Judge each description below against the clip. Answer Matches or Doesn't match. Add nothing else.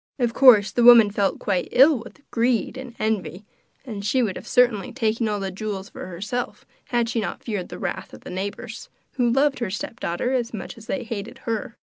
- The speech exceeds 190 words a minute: Matches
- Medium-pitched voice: Doesn't match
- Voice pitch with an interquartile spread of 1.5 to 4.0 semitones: Matches